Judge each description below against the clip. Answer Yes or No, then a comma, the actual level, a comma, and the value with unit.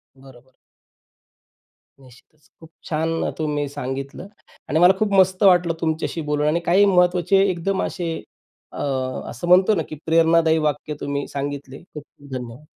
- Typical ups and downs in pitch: Yes, average, 3.8 semitones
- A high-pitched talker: No, medium, 160 Hz